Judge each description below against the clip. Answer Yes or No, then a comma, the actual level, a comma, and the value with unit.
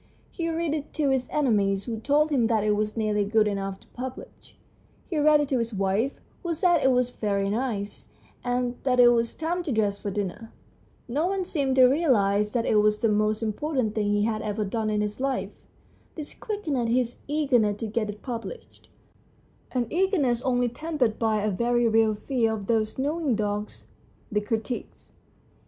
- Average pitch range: Yes, average, 4.5 semitones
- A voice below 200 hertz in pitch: No, high, 235 Hz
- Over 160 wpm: Yes, average, 190 wpm